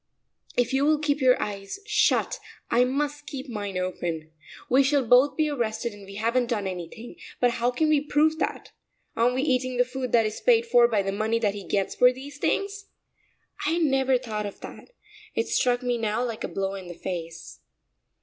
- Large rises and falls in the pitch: No, average, 5.0 semitones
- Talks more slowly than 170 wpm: No, fast, 205 wpm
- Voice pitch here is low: No, high, 245 Hz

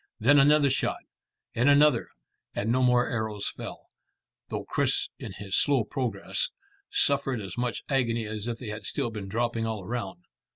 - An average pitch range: Yes, average, 3.7 semitones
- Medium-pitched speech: No, low, 120 Hz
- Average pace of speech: Yes, average, 165 wpm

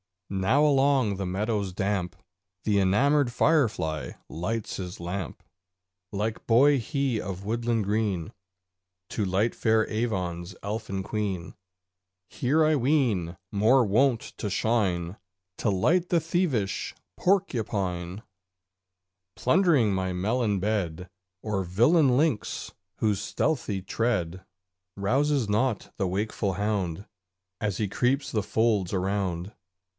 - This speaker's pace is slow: Yes, slow, 110 wpm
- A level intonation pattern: No, average, 4.5 semitones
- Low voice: Yes, low, 105 Hz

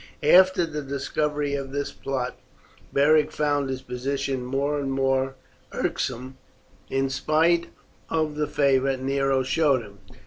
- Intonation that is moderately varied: No, narrow, 1.9 semitones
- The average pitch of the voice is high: No, medium, 140 Hz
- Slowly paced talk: Yes, slow, 130 wpm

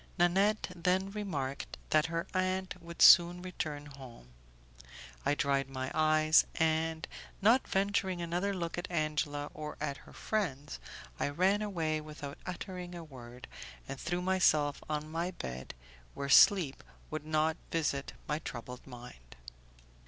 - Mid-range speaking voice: Yes, medium, 155 Hz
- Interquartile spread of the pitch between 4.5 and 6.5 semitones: No, average, 4.0 semitones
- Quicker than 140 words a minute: No, slow, 135 wpm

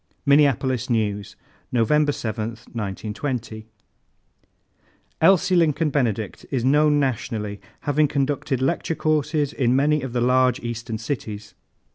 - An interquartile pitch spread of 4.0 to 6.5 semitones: Yes, average, 4.6 semitones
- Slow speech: Yes, slow, 110 wpm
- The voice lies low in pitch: Yes, low, 130 Hz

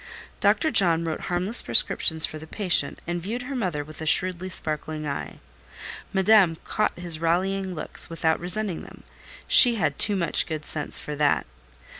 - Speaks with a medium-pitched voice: Yes, medium, 175 Hz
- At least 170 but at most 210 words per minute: No, average, 160 wpm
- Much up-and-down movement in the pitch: No, average, 3.6 semitones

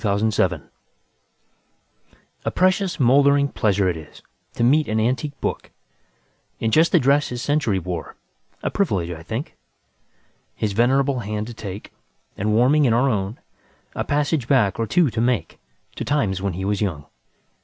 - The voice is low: Yes, low, 115 Hz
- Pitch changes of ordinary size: No, wide, 5.9 semitones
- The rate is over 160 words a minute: No, average, 145 wpm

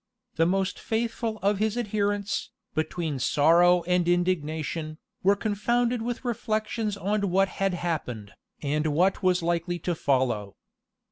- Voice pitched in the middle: Yes, medium, 180 Hz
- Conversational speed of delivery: No, slow, 130 wpm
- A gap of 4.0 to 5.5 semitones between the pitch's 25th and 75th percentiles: Yes, average, 4.6 semitones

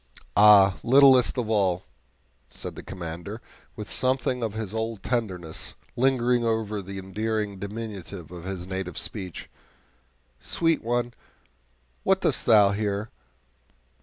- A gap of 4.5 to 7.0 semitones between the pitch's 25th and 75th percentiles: No, average, 3.7 semitones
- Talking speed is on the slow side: Yes, slow, 120 wpm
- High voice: No, low, 105 Hz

